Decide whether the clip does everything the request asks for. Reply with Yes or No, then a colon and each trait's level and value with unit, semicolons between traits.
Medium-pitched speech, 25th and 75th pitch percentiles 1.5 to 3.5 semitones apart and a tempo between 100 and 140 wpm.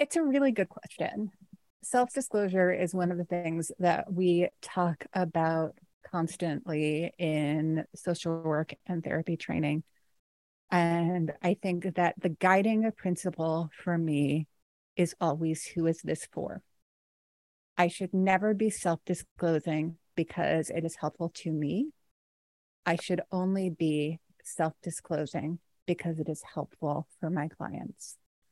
Yes: medium, 170 Hz; narrow, 2.5 semitones; slow, 135 wpm